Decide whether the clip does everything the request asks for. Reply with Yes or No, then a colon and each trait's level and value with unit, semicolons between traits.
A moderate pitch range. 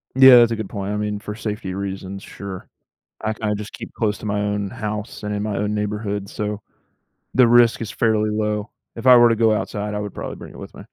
No: narrow, 1.3 semitones